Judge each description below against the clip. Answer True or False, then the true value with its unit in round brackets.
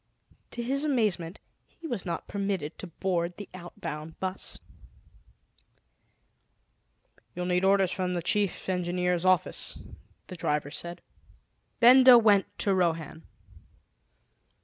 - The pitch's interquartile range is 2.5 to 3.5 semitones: True (2.9 semitones)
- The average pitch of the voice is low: False (185 Hz)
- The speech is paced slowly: True (110 wpm)